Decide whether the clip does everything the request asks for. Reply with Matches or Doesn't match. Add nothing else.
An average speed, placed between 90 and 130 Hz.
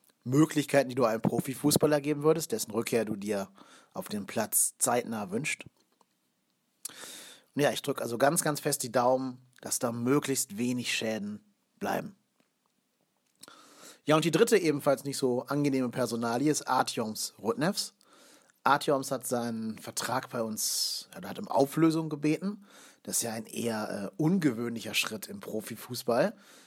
Doesn't match